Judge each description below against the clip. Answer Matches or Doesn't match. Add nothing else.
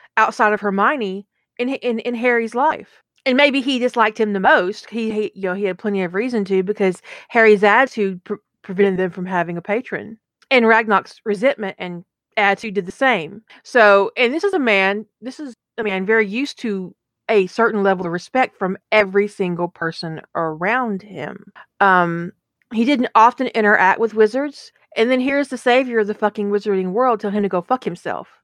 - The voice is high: Matches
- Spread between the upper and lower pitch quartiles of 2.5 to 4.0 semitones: Matches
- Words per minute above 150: Matches